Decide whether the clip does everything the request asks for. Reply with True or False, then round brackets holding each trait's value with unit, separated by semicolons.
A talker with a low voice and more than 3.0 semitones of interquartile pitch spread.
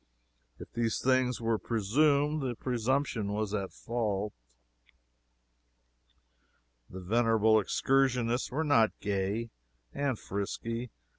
True (115 Hz; 3.4 semitones)